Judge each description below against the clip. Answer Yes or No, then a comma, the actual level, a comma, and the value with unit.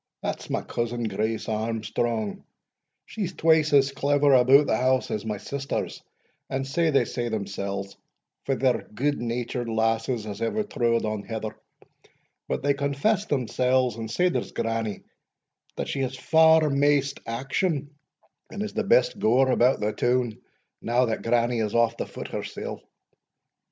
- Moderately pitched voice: No, low, 125 Hz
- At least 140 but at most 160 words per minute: Yes, average, 150 wpm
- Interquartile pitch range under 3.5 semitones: No, average, 3.8 semitones